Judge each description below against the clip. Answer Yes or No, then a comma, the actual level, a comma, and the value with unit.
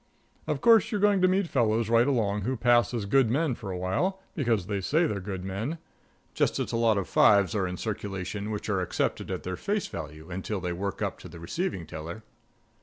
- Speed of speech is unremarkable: No, fast, 220 wpm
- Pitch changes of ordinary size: No, wide, 5.8 semitones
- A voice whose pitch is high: No, low, 105 Hz